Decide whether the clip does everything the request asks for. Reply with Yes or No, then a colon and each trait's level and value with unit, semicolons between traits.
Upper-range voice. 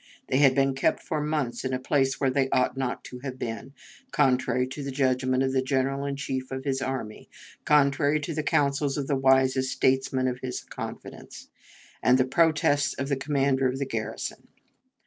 No: low, 135 Hz